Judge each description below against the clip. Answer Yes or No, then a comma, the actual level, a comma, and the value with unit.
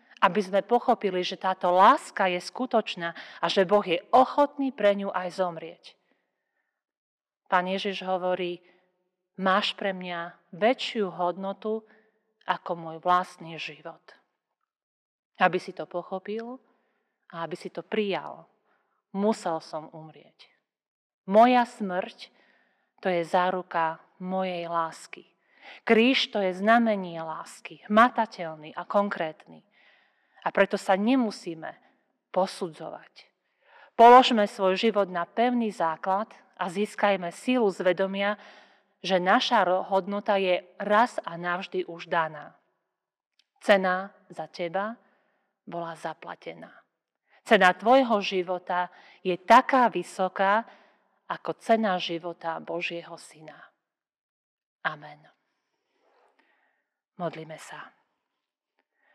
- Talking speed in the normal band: No, slow, 100 wpm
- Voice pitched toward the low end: No, high, 190 Hz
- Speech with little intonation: No, average, 3.1 semitones